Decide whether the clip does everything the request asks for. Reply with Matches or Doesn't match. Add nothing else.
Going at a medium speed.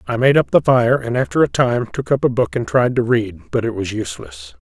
Doesn't match